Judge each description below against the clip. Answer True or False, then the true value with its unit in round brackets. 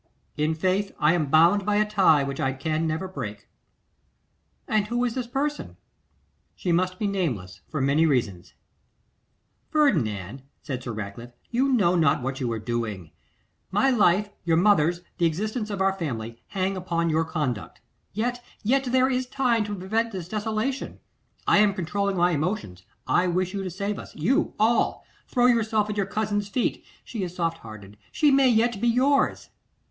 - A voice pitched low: False (185 Hz)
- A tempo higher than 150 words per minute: True (175 wpm)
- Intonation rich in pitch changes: True (6.3 semitones)